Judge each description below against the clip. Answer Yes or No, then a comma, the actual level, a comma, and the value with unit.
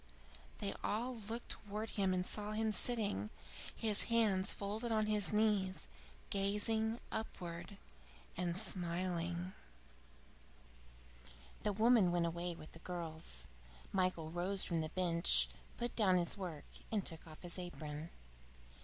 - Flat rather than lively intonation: No, average, 3.8 semitones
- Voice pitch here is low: No, medium, 185 Hz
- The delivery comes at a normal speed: No, slow, 130 wpm